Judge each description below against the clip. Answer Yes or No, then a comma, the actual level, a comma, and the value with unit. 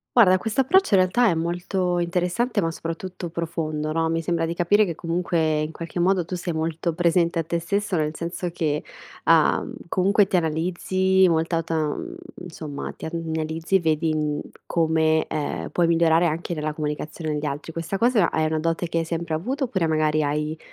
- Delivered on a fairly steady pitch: Yes, narrow, 2.2 semitones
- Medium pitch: Yes, medium, 165 Hz